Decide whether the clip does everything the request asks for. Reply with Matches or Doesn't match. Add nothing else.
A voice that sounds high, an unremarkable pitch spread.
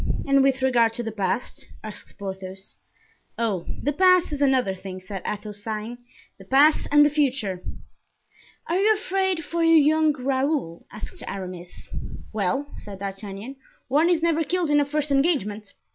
Doesn't match